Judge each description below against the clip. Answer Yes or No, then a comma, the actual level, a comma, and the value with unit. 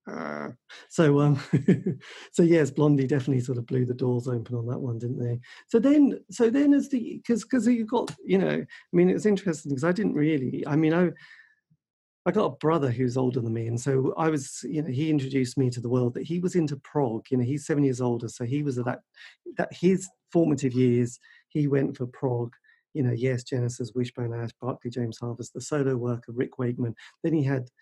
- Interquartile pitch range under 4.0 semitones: No, average, 5.0 semitones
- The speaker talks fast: Yes, fast, 220 wpm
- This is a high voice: No, low, 135 Hz